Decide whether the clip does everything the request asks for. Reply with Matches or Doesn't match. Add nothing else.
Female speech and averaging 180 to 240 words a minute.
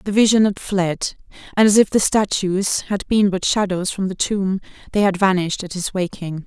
Matches